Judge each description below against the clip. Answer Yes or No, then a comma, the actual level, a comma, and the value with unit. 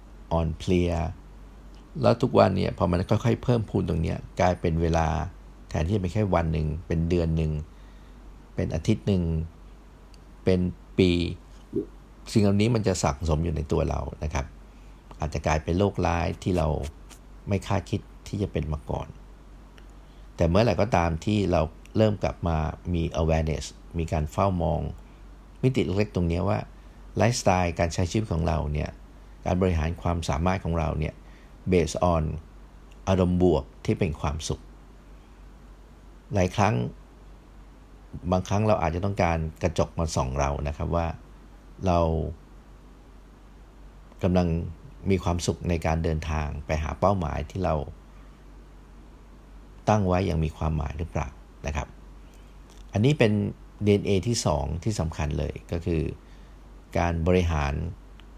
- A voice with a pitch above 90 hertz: No, very low, 85 Hz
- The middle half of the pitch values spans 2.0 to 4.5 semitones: Yes, average, 3.4 semitones